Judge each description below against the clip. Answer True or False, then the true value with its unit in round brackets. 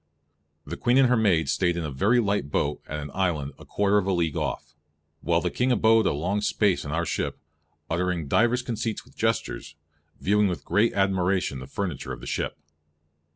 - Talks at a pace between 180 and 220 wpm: True (200 wpm)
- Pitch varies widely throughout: False (4.5 semitones)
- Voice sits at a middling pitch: False (95 Hz)